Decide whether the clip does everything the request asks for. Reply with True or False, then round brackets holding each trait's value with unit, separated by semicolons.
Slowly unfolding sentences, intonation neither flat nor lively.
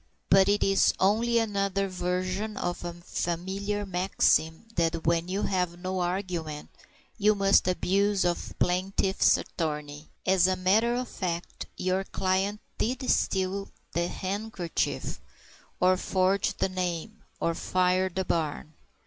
False (130 wpm; 2.2 semitones)